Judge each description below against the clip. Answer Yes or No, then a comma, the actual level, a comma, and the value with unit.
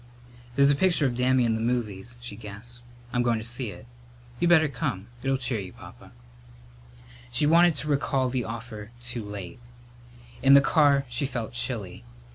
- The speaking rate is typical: Yes, average, 180 wpm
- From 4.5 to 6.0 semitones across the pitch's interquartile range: No, average, 3.6 semitones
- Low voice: Yes, low, 120 Hz